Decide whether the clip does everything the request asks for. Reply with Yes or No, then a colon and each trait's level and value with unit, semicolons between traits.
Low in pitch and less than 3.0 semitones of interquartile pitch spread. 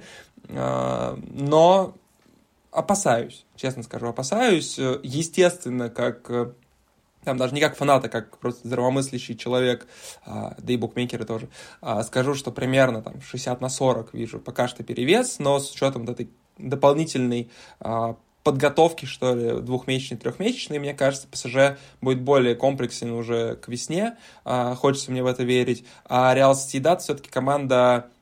Yes: low, 130 Hz; narrow, 2.6 semitones